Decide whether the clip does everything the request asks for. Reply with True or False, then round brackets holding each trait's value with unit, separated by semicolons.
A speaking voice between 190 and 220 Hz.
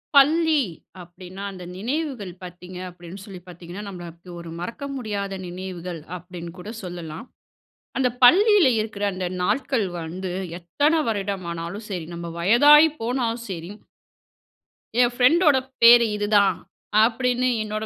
True (200 Hz)